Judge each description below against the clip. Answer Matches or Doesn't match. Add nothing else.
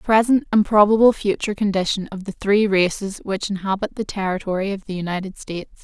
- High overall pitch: Matches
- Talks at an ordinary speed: Matches